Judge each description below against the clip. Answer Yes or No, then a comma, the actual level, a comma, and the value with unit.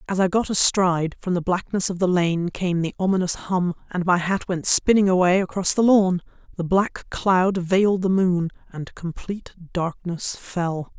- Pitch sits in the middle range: Yes, medium, 180 Hz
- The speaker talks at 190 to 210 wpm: No, average, 175 wpm